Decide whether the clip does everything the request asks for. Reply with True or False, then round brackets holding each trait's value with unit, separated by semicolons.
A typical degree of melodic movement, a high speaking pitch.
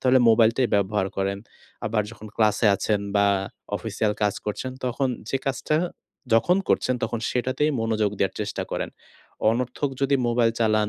False (3.3 semitones; 115 Hz)